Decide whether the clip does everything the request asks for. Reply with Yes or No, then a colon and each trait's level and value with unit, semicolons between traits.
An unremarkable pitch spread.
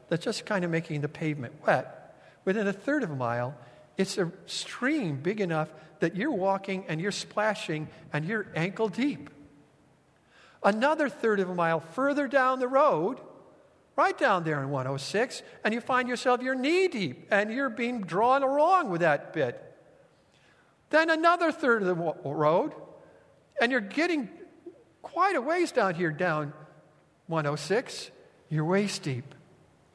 No: wide, 8.9 semitones